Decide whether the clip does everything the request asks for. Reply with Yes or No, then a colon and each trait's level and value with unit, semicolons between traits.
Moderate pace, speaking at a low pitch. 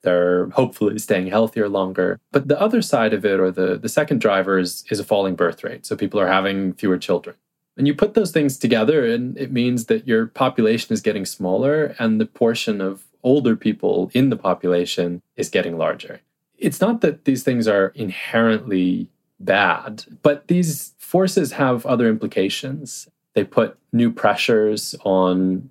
Yes: average, 175 wpm; low, 115 Hz